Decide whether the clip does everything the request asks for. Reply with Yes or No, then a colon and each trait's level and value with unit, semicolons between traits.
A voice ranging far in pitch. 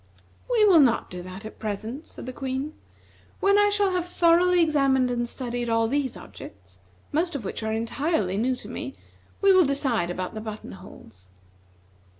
Yes: wide, 7.3 semitones